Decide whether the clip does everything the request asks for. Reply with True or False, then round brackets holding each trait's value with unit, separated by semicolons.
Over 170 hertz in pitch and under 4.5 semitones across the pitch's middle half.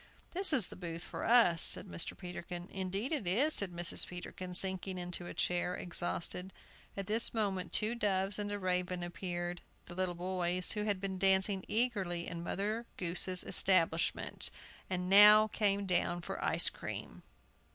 True (185 Hz; 2.5 semitones)